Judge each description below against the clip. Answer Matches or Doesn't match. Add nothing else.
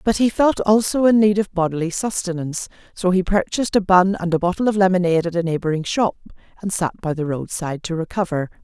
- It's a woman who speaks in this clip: Matches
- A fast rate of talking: Matches